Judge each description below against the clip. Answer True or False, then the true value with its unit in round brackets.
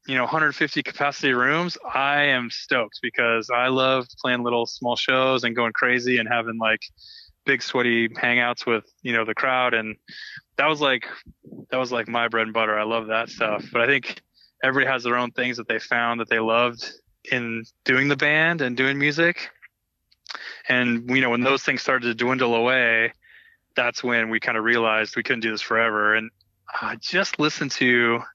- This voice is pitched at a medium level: False (120 Hz)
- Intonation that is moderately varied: False (2.3 semitones)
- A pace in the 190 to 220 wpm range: True (195 wpm)